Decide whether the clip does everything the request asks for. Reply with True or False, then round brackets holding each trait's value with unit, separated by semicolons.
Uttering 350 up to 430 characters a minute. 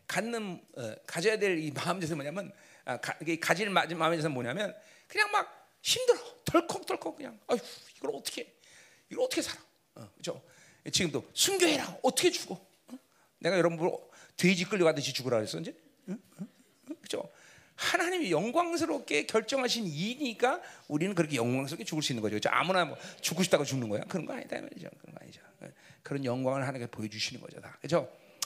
True (365 characters per minute)